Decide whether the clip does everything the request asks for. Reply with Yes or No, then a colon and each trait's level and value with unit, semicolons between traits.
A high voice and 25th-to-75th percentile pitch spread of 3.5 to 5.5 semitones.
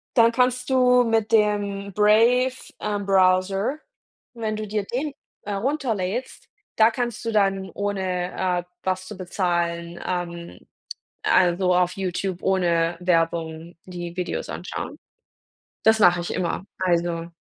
Yes: high, 195 Hz; average, 3.9 semitones